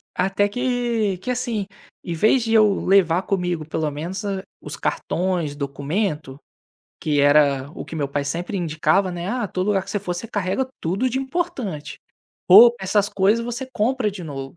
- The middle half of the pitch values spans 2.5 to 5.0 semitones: No, wide, 5.6 semitones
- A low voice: No, high, 190 Hz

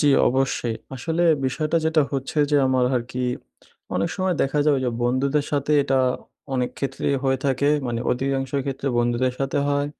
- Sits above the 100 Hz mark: Yes, low, 135 Hz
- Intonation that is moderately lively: No, narrow, 2.2 semitones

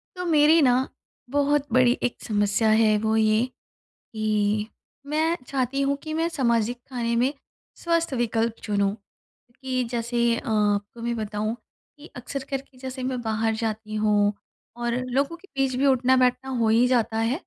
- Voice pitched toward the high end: Yes, high, 240 Hz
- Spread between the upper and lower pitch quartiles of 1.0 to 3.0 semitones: No, average, 3.7 semitones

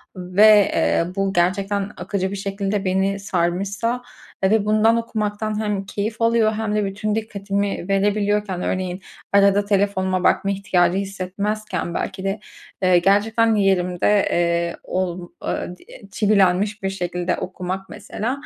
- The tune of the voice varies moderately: No, narrow, 2.0 semitones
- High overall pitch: Yes, high, 195 Hz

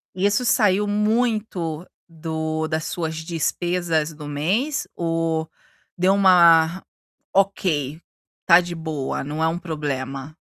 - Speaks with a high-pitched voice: No, medium, 165 Hz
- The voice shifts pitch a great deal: No, average, 3.1 semitones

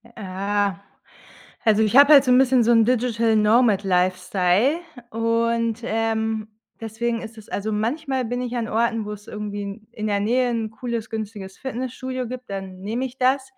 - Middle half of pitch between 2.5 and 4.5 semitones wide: Yes, average, 2.9 semitones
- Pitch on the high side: Yes, high, 225 Hz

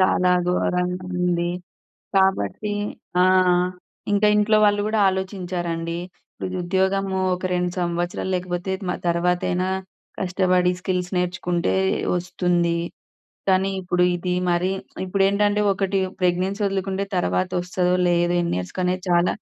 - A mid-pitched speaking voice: Yes, medium, 180 Hz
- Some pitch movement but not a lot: No, narrow, 1.4 semitones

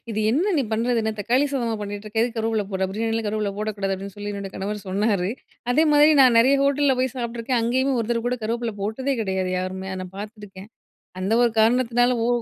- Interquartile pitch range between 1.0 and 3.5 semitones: Yes, average, 3.2 semitones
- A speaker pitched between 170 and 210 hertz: No, high, 225 Hz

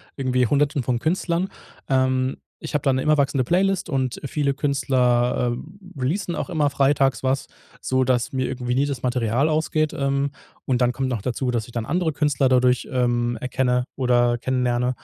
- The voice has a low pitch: Yes, low, 130 Hz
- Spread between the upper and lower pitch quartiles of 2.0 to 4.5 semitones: Yes, narrow, 2.5 semitones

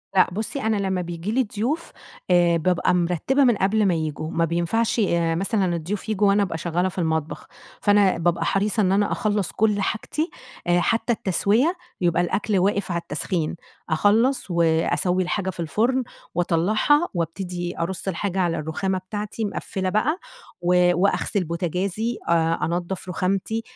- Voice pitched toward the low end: No, medium, 185 Hz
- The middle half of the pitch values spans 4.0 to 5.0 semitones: No, average, 3.5 semitones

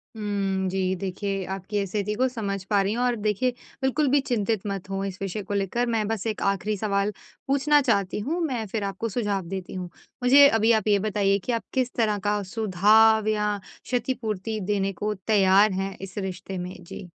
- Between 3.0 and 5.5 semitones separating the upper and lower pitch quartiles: No, narrow, 2.5 semitones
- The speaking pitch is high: Yes, high, 205 Hz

